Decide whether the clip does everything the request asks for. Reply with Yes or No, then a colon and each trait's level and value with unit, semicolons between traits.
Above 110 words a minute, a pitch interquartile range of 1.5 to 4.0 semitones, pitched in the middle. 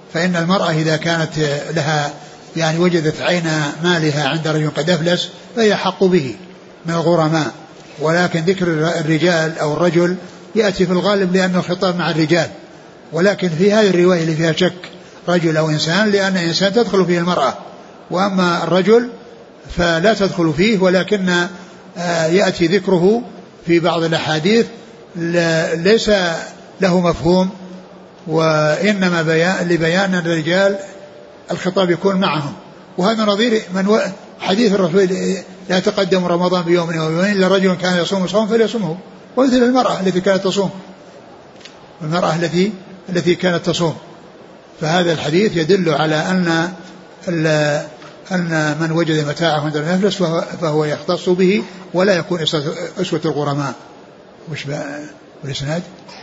Yes: average, 120 wpm; average, 2.7 semitones; medium, 175 Hz